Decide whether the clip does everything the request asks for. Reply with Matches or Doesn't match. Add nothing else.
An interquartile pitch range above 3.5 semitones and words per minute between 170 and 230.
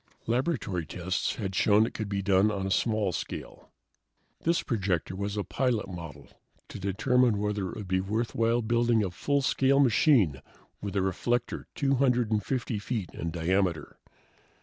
Doesn't match